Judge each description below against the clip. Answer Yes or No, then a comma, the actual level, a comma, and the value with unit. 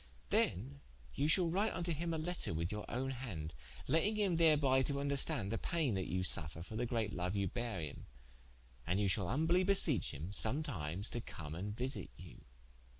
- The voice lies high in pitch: No, low, 120 Hz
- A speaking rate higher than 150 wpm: Yes, average, 195 wpm